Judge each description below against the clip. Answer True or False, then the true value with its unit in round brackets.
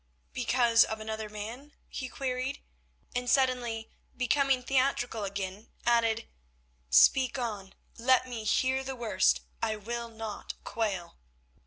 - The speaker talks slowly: True (120 wpm)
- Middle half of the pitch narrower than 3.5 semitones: True (2.9 semitones)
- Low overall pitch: False (235 Hz)